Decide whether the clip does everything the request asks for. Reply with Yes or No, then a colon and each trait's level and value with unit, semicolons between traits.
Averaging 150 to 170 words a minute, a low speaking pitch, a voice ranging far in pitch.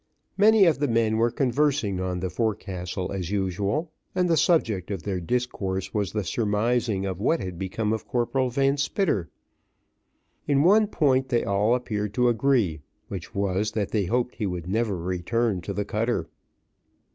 No: average, 165 wpm; low, 110 Hz; average, 4.6 semitones